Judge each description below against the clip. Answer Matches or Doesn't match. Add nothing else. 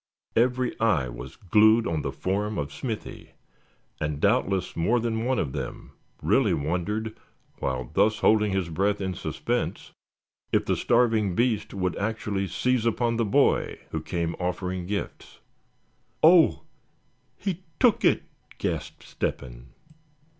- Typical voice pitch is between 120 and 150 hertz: Doesn't match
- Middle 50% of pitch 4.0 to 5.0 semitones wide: Matches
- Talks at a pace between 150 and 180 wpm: Doesn't match